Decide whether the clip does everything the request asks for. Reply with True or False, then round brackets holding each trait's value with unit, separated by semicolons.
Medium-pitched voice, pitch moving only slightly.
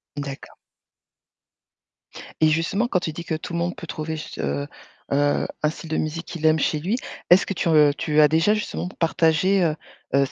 True (160 Hz; 2.3 semitones)